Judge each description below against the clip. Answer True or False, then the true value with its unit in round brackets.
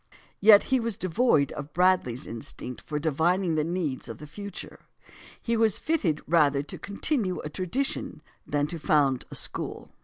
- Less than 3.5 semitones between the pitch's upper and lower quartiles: False (5.4 semitones)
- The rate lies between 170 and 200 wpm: False (160 wpm)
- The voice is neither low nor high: True (170 Hz)